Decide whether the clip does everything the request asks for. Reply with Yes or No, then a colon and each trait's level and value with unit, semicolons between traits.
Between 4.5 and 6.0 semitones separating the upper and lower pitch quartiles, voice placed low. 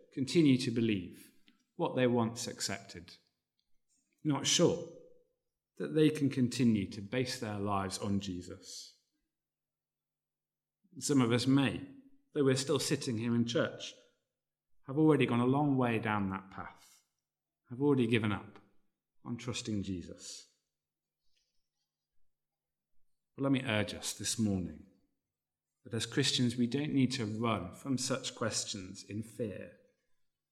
Yes: average, 4.9 semitones; low, 120 Hz